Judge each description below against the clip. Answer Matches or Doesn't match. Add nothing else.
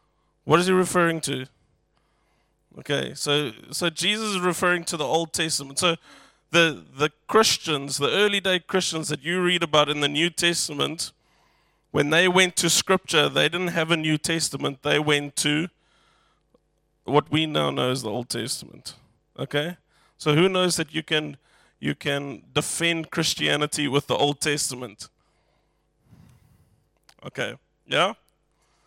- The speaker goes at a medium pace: Matches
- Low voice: Doesn't match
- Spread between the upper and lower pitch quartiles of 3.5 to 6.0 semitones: Doesn't match